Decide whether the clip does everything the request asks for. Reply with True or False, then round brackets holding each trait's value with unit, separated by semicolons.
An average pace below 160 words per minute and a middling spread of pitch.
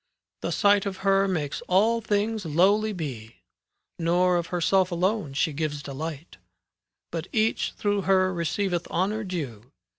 True (145 wpm; 4.0 semitones)